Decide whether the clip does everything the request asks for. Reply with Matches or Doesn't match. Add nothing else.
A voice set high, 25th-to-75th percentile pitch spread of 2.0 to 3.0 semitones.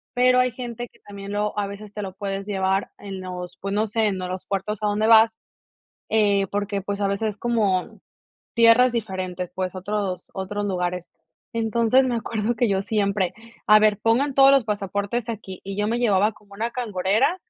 Matches